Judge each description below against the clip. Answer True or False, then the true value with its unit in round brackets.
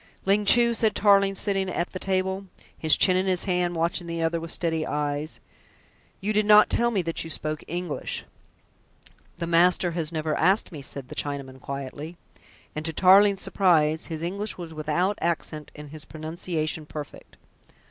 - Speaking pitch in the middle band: True (170 Hz)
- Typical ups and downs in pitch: True (3.6 semitones)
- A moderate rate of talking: True (170 wpm)